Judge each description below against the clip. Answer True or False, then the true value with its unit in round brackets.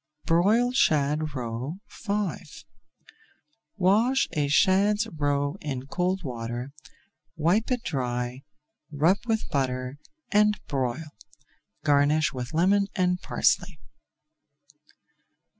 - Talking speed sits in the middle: False (90 wpm)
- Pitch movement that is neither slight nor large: False (6.2 semitones)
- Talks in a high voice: False (155 Hz)